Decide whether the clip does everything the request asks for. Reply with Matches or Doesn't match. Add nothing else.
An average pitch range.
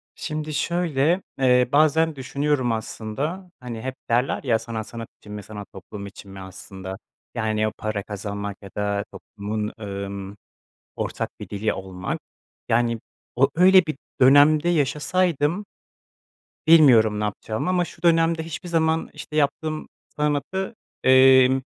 Doesn't match